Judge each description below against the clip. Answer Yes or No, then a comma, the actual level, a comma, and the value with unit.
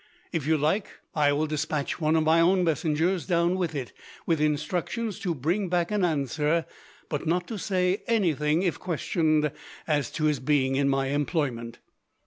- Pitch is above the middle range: No, medium, 160 Hz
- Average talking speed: Yes, average, 170 wpm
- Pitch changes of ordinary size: Yes, average, 3.2 semitones